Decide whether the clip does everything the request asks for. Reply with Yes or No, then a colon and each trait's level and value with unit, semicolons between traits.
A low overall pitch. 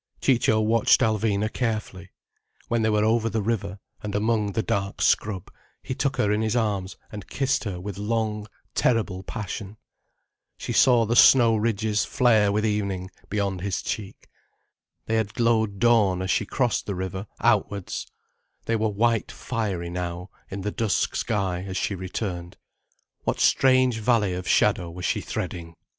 Yes: low, 105 Hz